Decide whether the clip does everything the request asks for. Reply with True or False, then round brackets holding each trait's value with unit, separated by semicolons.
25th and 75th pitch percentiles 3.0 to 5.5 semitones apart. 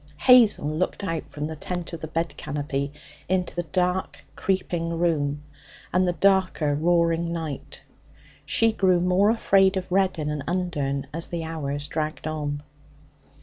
True (3.5 semitones)